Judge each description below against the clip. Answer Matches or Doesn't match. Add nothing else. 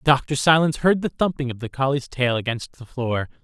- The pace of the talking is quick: Matches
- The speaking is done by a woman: Doesn't match